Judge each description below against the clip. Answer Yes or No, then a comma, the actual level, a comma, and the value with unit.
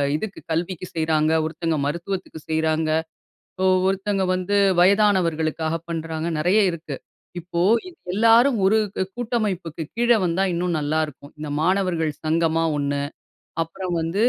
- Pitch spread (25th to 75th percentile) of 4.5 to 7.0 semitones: No, average, 3.4 semitones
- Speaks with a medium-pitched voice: Yes, medium, 170 Hz